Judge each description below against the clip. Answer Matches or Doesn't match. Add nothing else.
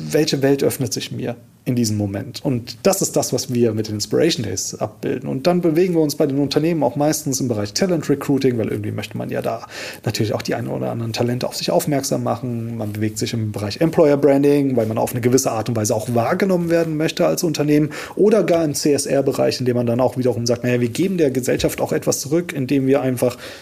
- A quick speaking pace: Matches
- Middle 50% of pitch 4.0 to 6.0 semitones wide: Matches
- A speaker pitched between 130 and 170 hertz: Matches